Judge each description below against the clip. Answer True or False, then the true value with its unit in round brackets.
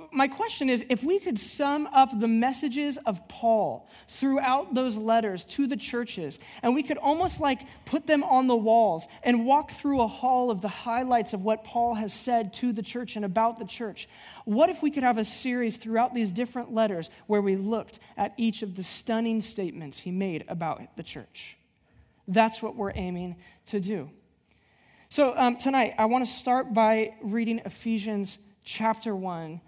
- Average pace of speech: True (185 wpm)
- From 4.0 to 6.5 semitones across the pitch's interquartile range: False (3.5 semitones)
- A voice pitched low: False (230 Hz)